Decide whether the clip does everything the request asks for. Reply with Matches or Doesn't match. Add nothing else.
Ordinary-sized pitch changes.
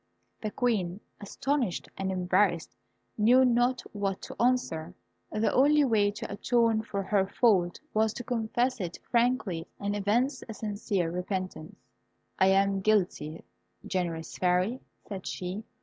Matches